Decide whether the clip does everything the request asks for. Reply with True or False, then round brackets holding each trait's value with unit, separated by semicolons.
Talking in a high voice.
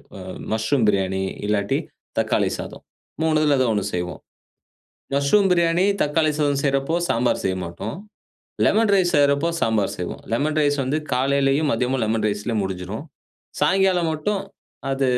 False (135 Hz)